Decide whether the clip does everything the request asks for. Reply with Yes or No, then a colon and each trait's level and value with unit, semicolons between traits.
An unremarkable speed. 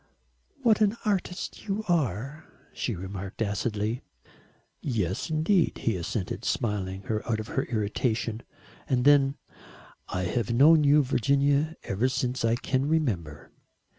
No: slow, 130 wpm